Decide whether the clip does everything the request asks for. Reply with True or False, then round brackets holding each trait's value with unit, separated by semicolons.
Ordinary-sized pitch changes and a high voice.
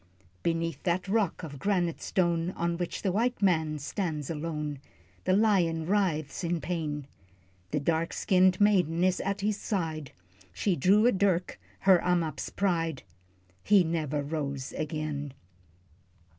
False (3.6 semitones; 170 Hz)